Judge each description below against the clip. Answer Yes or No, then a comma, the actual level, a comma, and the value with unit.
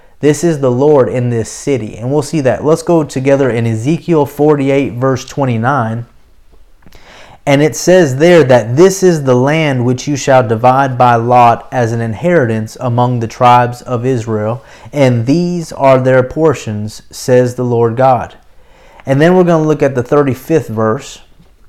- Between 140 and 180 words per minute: Yes, average, 170 wpm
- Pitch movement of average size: Yes, average, 3.8 semitones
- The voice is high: No, low, 130 Hz